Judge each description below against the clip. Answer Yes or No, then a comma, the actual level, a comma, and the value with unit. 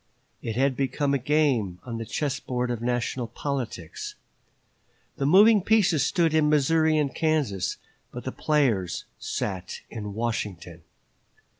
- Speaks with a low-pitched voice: Yes, low, 130 Hz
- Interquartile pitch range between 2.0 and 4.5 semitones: No, average, 5.1 semitones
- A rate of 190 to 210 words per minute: No, slow, 135 wpm